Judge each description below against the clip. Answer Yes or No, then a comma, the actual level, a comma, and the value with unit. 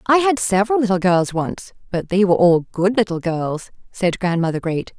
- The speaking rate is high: No, average, 195 wpm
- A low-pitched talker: No, high, 195 Hz